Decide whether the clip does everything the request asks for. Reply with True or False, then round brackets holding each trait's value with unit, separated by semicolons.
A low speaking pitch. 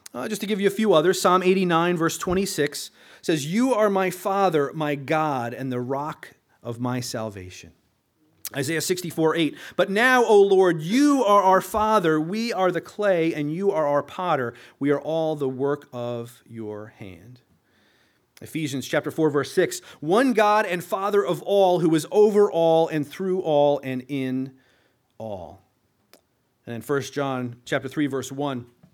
False (155 Hz)